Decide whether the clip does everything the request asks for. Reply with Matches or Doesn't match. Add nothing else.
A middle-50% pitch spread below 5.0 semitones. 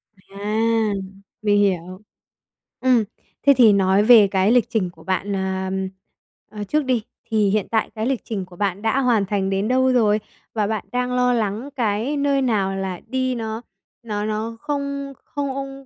Matches